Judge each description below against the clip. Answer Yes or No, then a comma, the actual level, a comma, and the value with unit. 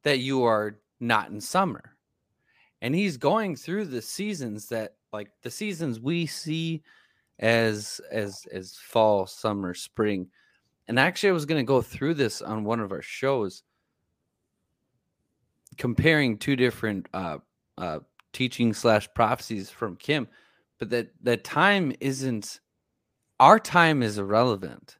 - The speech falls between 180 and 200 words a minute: No, slow, 135 wpm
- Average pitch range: No, wide, 6.5 semitones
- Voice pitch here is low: Yes, low, 120 Hz